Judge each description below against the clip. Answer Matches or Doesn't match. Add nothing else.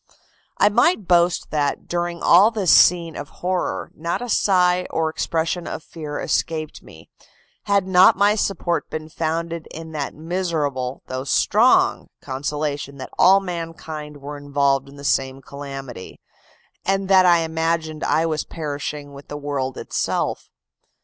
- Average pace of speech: Matches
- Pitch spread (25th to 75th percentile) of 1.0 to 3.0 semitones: Doesn't match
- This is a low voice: Doesn't match